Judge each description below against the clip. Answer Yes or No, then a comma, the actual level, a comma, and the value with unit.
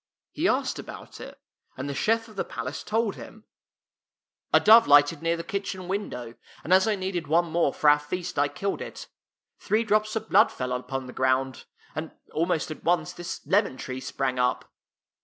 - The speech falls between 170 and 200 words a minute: Yes, average, 195 wpm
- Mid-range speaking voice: Yes, medium, 165 Hz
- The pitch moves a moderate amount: No, wide, 6.7 semitones